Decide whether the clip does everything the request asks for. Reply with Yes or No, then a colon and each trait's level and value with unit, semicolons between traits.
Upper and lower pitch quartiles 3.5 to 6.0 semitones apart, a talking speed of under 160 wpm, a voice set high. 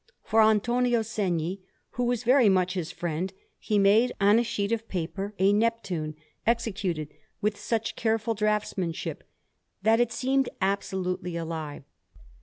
Yes: average, 4.0 semitones; slow, 135 wpm; high, 205 Hz